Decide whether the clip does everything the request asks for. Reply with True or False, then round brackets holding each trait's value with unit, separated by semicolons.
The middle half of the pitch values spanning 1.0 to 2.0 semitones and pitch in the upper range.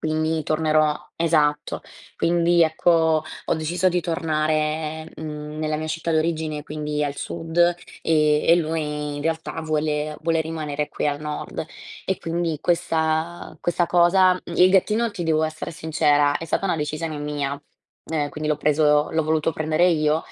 False (1.5 semitones; 155 Hz)